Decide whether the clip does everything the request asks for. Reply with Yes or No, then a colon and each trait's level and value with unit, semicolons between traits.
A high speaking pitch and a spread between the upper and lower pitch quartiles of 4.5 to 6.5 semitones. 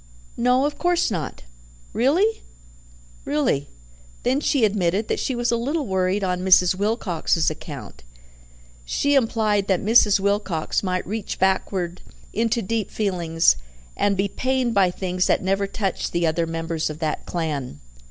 Yes: high, 195 Hz; average, 4.9 semitones